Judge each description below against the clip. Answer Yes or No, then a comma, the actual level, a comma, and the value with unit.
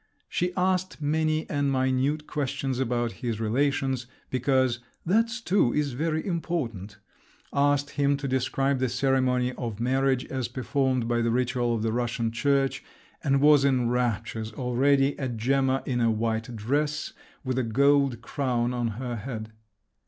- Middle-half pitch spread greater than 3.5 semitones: No, average, 2.9 semitones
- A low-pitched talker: Yes, low, 130 Hz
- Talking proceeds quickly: No, average, 150 wpm